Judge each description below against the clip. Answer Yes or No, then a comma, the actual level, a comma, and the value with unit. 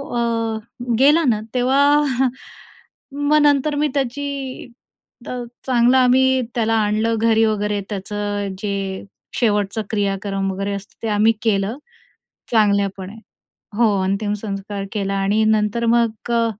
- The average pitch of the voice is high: Yes, high, 220 Hz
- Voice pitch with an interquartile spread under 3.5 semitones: No, average, 3.8 semitones